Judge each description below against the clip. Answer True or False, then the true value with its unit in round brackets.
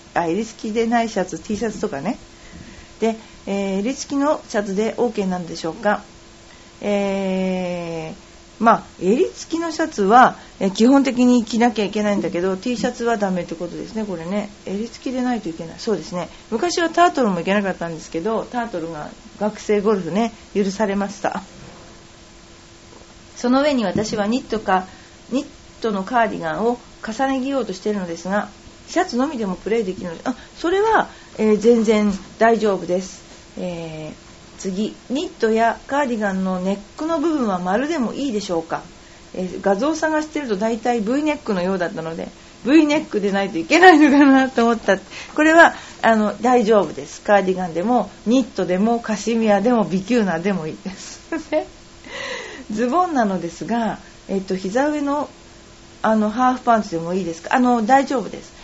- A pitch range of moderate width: True (4.8 semitones)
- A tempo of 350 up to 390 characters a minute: True (355 characters per minute)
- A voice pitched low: False (220 Hz)